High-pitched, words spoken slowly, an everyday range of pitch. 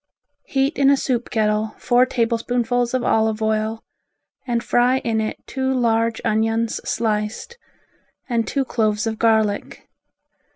No: high, 230 Hz; slow, 130 wpm; narrow, 2.1 semitones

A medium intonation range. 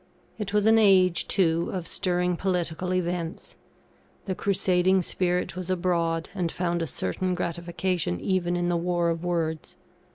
No: narrow, 1.5 semitones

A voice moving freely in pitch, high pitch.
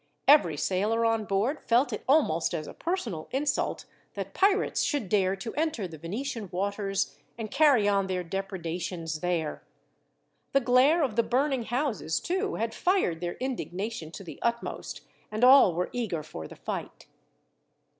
Yes: wide, 6.9 semitones; high, 215 Hz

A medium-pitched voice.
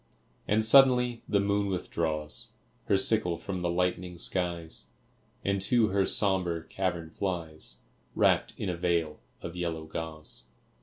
No: very low, 90 Hz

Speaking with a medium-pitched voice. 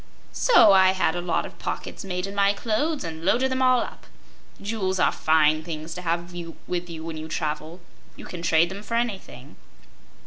Yes: medium, 180 Hz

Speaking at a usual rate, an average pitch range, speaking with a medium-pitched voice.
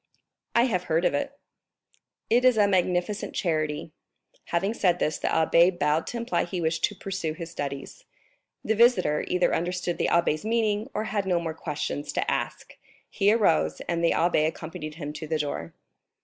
Yes: average, 175 wpm; average, 4.7 semitones; medium, 175 Hz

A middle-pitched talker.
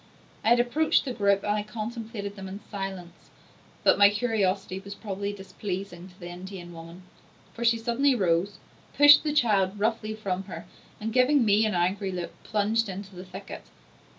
No: high, 200 Hz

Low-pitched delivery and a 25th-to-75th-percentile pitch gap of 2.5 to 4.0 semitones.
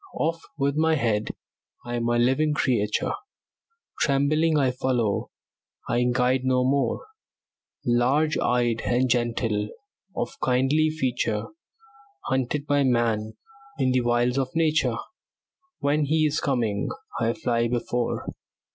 Yes: low, 125 Hz; average, 3.2 semitones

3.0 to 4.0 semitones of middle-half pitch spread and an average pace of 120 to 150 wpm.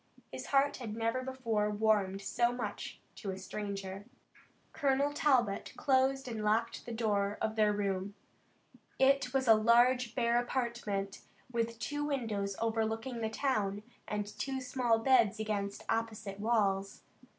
Yes: average, 3.5 semitones; average, 140 wpm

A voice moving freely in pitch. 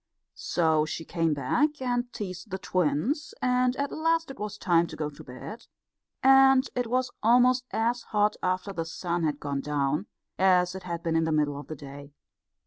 Yes: wide, 7.9 semitones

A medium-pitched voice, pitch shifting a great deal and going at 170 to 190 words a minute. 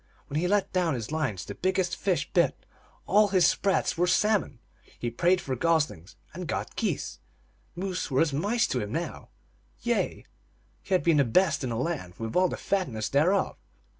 Yes: medium, 170 Hz; wide, 6.0 semitones; average, 185 wpm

